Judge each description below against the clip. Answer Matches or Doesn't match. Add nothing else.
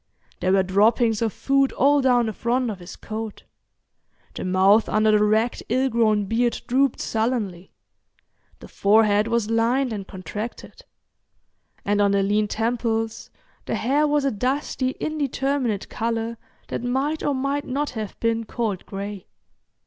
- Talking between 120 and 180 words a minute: Matches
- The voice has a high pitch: Matches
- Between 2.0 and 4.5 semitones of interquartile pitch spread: Matches